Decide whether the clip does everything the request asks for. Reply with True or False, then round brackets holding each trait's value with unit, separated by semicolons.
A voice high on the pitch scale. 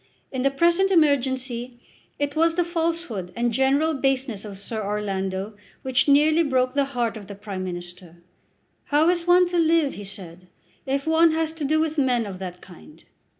True (265 Hz)